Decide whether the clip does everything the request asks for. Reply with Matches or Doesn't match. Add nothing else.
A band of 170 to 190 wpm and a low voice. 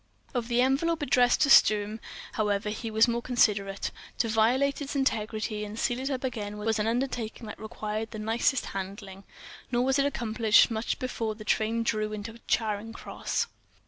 Doesn't match